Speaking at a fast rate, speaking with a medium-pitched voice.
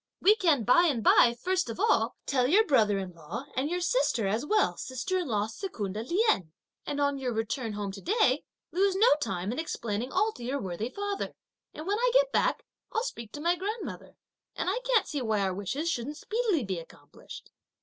No: fast, 210 wpm; very high, 275 Hz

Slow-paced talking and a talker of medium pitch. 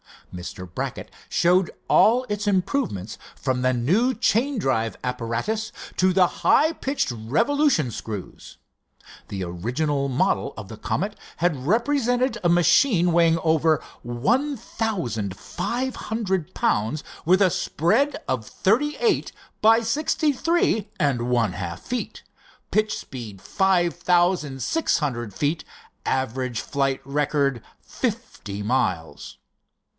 Yes: slow, 120 wpm; medium, 165 Hz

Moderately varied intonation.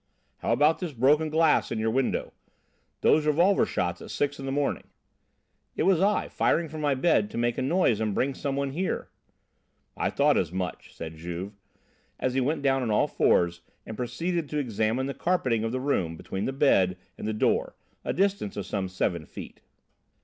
No: wide, 6.3 semitones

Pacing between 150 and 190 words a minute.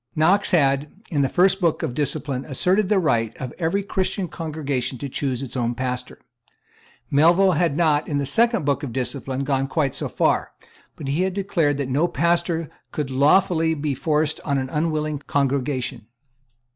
Yes: average, 170 wpm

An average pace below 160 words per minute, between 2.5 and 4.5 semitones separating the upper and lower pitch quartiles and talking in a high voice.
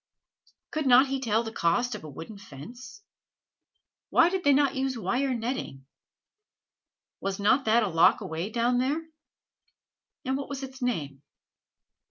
No: average, 150 wpm; average, 5.2 semitones; high, 245 Hz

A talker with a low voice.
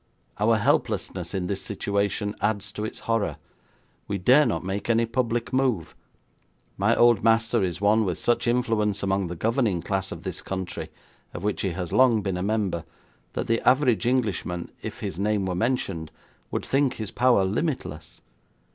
Yes: low, 105 Hz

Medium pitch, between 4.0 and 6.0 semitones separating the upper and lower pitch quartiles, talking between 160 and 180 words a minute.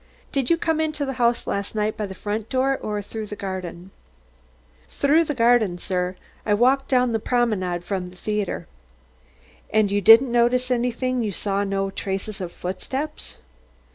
No: high, 215 Hz; average, 4.5 semitones; average, 170 wpm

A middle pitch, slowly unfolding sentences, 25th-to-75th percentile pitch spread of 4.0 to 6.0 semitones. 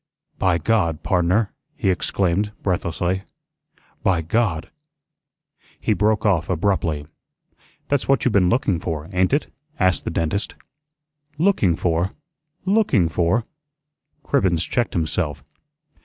No: very low, 95 Hz; slow, 115 wpm; average, 4.3 semitones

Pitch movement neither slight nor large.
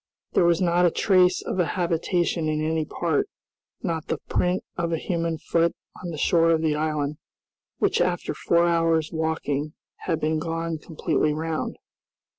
No: narrow, 1.6 semitones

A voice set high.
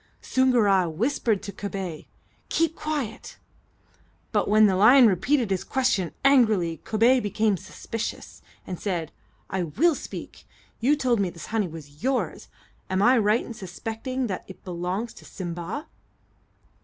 Yes: high, 210 Hz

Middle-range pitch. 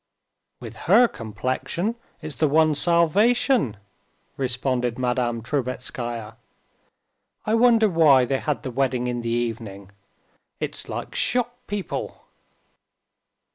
No: low, 130 Hz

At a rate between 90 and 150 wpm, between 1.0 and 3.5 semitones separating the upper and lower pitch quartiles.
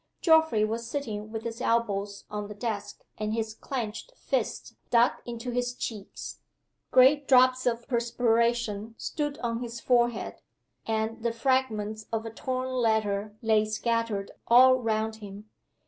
Yes: average, 140 wpm; narrow, 2.4 semitones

